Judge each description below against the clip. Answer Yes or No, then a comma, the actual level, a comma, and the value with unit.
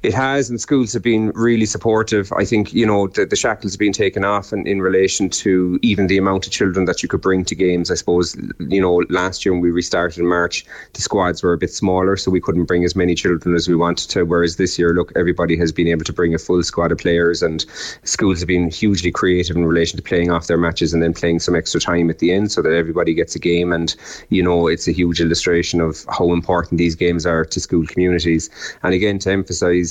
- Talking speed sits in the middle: No, fast, 250 wpm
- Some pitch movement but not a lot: No, narrow, 2.2 semitones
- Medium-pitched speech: No, very low, 90 Hz